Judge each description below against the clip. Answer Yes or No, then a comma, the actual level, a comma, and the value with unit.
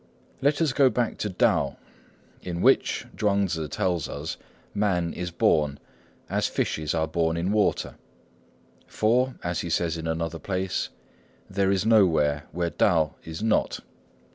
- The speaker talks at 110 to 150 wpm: Yes, average, 145 wpm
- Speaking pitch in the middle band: No, very low, 90 Hz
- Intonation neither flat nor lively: Yes, average, 4.0 semitones